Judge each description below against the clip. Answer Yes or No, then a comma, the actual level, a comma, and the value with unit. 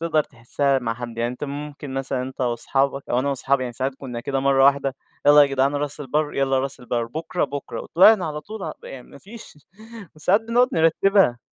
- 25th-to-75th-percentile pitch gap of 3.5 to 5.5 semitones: No, narrow, 2.6 semitones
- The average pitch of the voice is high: No, medium, 140 Hz